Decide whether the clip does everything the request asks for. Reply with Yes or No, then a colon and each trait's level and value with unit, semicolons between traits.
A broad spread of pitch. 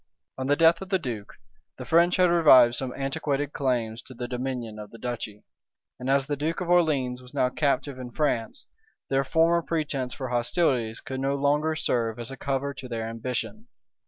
No: average, 3.8 semitones